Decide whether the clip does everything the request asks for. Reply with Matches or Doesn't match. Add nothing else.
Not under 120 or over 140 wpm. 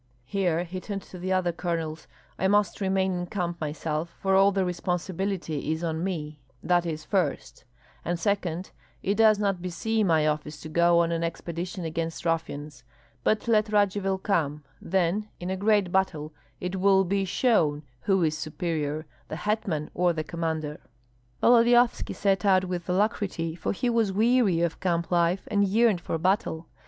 Doesn't match